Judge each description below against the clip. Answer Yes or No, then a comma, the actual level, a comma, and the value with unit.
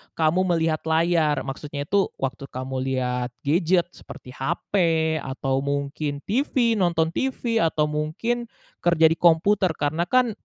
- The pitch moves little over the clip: No, average, 4.0 semitones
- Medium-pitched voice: Yes, medium, 160 Hz